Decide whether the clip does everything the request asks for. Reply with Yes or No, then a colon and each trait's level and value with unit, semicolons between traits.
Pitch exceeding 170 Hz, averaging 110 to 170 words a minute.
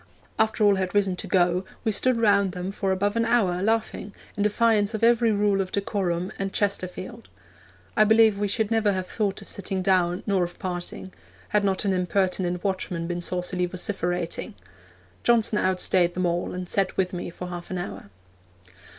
No: high, 190 Hz; average, 180 wpm